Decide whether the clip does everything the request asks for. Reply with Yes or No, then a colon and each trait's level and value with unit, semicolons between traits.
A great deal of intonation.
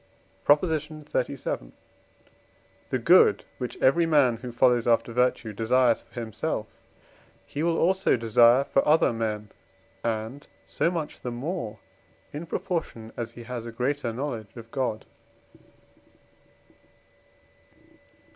No: average, 4.4 semitones